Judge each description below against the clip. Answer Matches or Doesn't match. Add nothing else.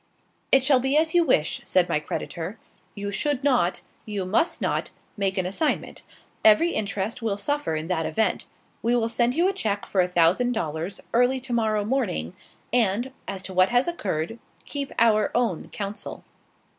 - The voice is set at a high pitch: Matches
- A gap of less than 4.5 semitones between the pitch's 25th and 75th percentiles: Doesn't match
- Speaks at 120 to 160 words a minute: Doesn't match